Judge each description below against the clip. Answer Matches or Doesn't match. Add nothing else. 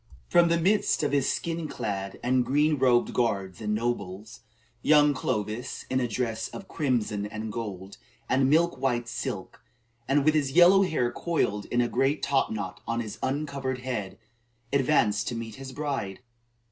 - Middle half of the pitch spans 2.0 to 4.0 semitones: Doesn't match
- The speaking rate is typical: Matches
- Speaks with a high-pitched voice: Doesn't match